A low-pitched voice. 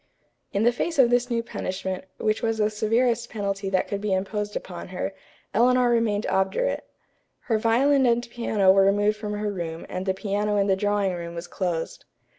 No: high, 210 Hz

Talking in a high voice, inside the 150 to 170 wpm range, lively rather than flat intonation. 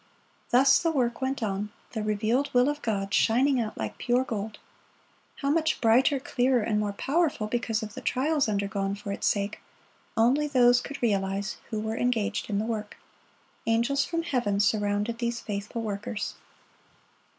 No: high, 225 Hz; average, 160 wpm; average, 3.9 semitones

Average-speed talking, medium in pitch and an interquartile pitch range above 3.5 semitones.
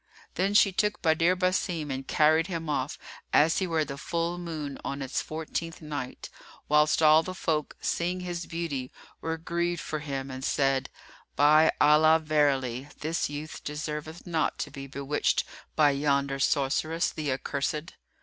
No: average, 160 wpm; medium, 155 Hz; average, 3.0 semitones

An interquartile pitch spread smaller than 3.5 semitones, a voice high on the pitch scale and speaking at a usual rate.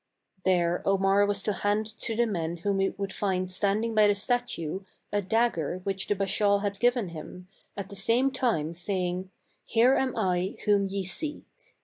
Yes: average, 2.7 semitones; high, 200 Hz; average, 175 wpm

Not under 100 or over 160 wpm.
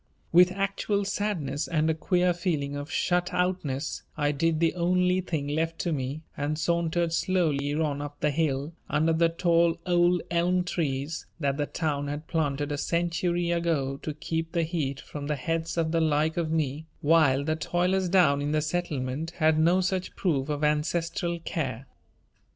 No: average, 175 wpm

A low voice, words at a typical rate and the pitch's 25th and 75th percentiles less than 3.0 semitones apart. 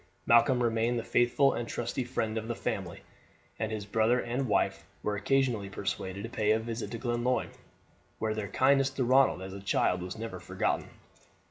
Yes: low, 115 Hz; average, 190 wpm; narrow, 2.5 semitones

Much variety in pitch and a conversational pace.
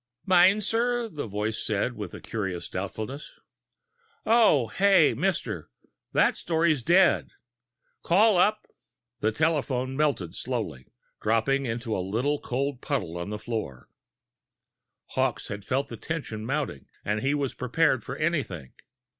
No: wide, 7.3 semitones; slow, 130 wpm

